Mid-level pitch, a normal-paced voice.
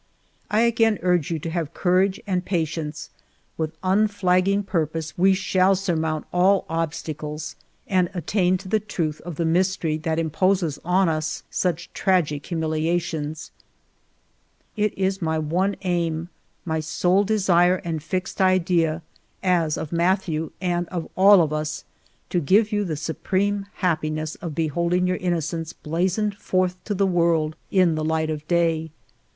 Yes: medium, 175 Hz; average, 150 wpm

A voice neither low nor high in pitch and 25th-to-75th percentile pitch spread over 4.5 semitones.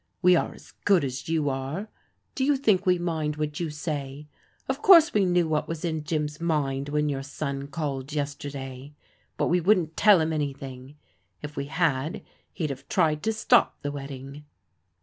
No: medium, 150 Hz; average, 3.5 semitones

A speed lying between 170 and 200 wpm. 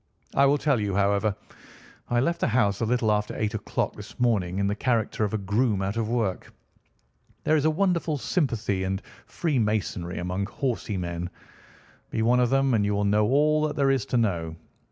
Yes: average, 195 wpm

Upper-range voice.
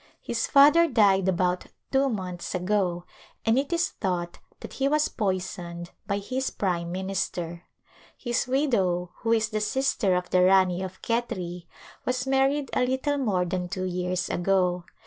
Yes: high, 195 Hz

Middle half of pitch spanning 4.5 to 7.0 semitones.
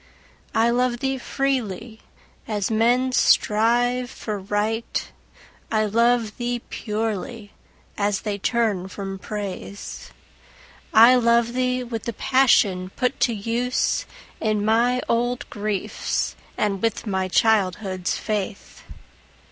No: average, 2.9 semitones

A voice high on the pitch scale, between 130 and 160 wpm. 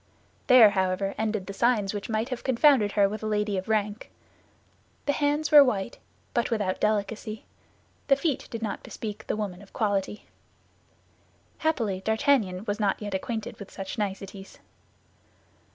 Yes: high, 210 Hz; average, 150 wpm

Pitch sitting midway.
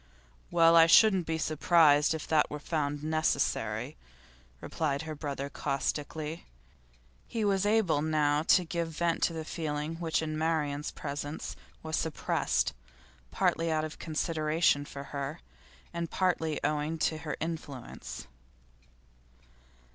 Yes: medium, 155 Hz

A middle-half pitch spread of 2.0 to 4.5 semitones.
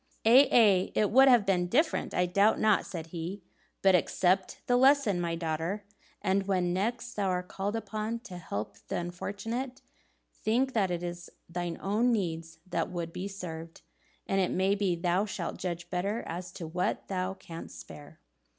Yes: average, 3.4 semitones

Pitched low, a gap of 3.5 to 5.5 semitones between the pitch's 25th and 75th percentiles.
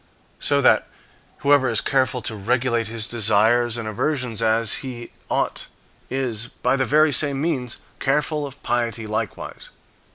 No: low, 120 Hz; average, 3.0 semitones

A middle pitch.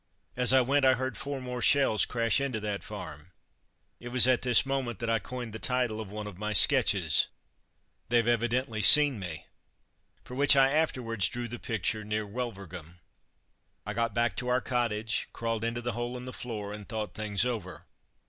No: low, 115 Hz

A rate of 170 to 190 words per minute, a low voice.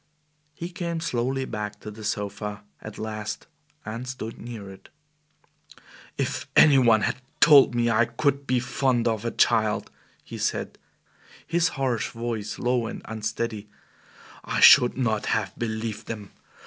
No: average, 145 wpm; low, 115 Hz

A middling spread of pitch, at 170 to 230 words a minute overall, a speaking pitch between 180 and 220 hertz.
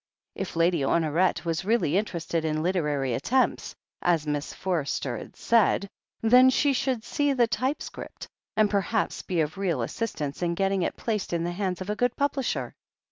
No: wide, 5.9 semitones; average, 175 wpm; medium, 185 Hz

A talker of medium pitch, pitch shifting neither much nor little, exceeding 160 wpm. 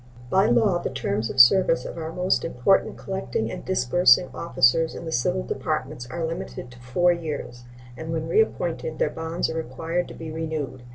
No: medium, 160 Hz; wide, 5.8 semitones; average, 180 wpm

